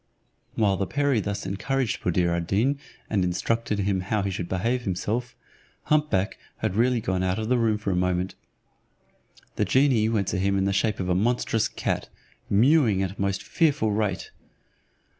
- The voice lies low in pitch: Yes, low, 105 Hz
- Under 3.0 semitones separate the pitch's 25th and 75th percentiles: No, average, 3.7 semitones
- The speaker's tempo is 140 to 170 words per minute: No, average, 180 wpm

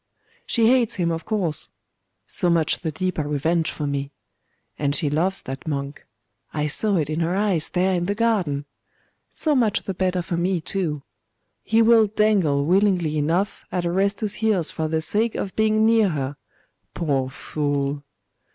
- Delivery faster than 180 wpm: No, average, 165 wpm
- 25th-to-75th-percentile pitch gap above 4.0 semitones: Yes, average, 5.3 semitones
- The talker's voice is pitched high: No, medium, 175 Hz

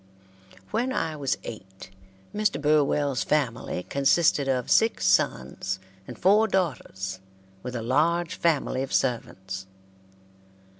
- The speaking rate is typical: No, slow, 110 wpm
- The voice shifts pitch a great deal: Yes, wide, 8.8 semitones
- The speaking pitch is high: No, low, 135 Hz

